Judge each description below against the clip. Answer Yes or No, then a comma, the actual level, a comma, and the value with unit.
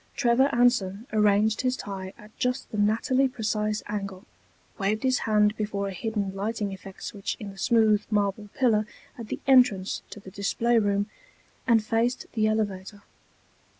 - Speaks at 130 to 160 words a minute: Yes, average, 155 wpm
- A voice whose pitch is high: Yes, high, 215 Hz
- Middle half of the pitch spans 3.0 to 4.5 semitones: No, narrow, 2.5 semitones